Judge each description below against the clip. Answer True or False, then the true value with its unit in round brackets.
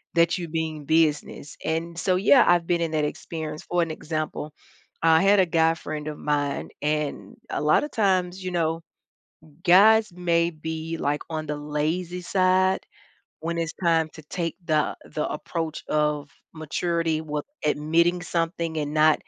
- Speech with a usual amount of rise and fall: False (2.2 semitones)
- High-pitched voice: False (165 Hz)